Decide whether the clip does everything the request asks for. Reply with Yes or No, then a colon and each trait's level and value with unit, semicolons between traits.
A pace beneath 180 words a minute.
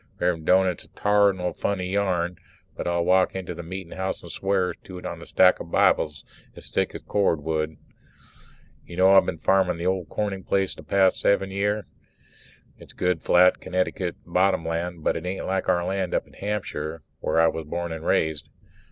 No: average, 200 wpm